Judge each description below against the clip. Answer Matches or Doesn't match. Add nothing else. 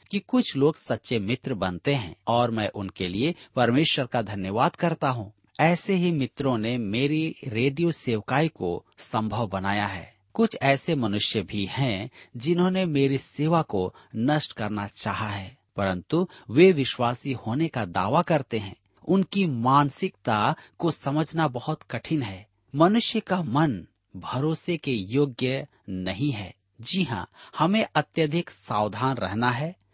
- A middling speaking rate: Matches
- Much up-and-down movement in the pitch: Matches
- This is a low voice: Matches